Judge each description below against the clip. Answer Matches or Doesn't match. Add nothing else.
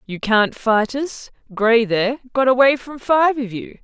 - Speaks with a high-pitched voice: Matches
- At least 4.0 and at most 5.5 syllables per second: Matches